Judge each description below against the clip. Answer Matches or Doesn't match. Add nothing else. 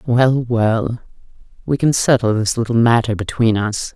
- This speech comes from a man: Doesn't match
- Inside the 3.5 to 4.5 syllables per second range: Matches